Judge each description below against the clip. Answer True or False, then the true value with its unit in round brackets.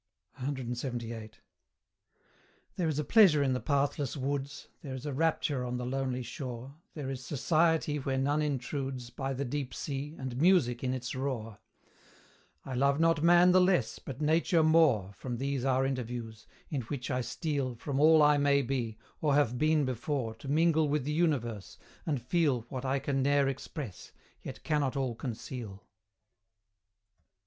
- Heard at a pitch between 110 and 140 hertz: True (135 Hz)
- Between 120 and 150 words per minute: False (160 wpm)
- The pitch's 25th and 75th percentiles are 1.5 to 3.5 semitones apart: True (3.0 semitones)